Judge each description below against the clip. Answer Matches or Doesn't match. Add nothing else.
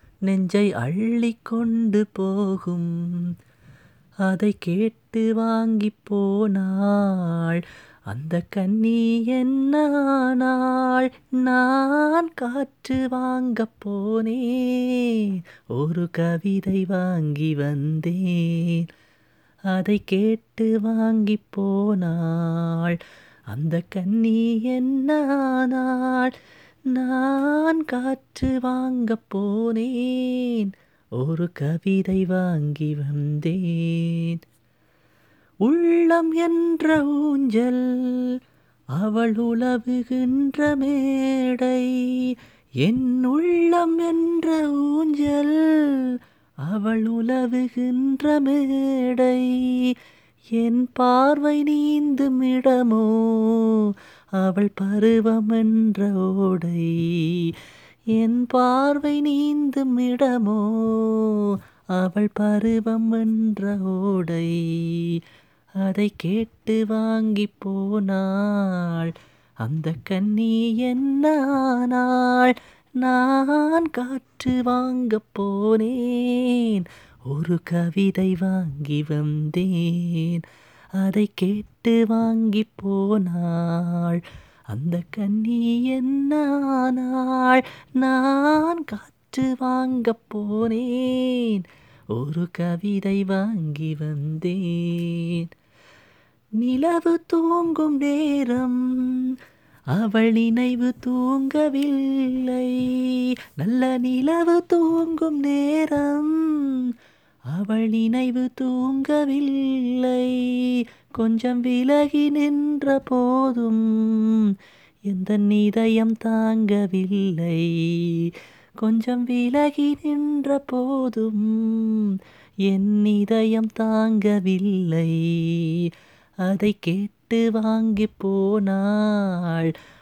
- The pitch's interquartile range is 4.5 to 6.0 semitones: Matches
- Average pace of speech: Doesn't match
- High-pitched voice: Matches